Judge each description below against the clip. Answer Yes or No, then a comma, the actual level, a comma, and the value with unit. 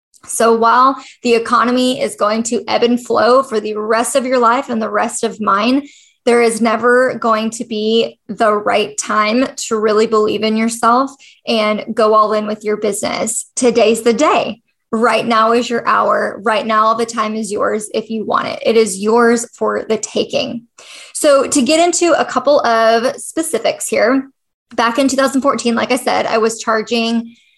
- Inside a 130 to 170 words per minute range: No, average, 185 wpm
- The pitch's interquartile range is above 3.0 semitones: No, average, 2.7 semitones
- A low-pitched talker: No, high, 230 Hz